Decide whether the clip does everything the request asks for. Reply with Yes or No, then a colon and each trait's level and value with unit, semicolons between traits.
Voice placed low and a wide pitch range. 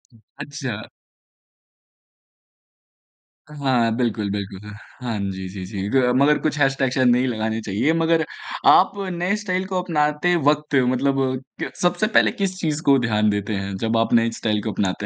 Yes: low, 125 Hz; wide, 6.0 semitones